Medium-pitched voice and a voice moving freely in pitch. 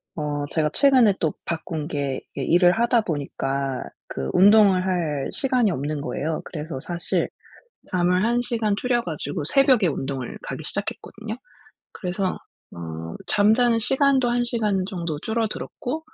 Yes: medium, 180 Hz; wide, 7.5 semitones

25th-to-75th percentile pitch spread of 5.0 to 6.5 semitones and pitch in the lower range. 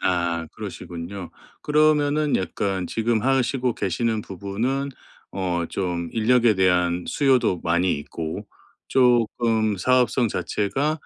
Yes: wide, 5.9 semitones; low, 110 Hz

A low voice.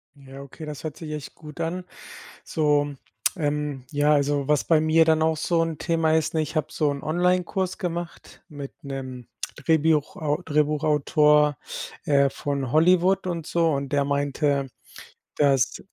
No: medium, 150 Hz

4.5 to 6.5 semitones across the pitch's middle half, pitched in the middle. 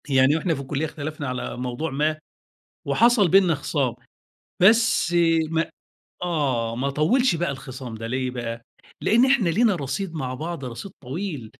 Yes: average, 5.2 semitones; medium, 150 Hz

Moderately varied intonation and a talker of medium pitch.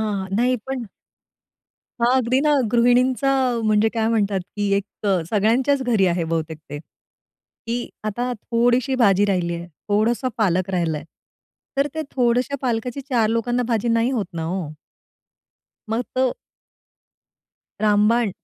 No: average, 3.7 semitones; high, 225 Hz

